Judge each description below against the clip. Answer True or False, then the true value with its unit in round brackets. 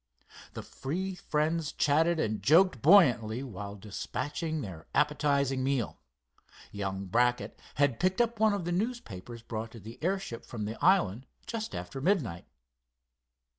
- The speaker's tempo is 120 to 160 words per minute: True (135 wpm)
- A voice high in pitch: False (140 Hz)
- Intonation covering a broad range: True (7.7 semitones)